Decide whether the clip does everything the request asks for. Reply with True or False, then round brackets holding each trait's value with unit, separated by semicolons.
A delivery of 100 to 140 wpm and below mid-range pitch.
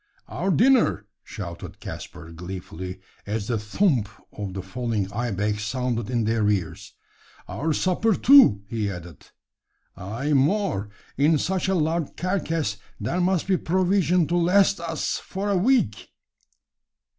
True (135 wpm; 125 Hz)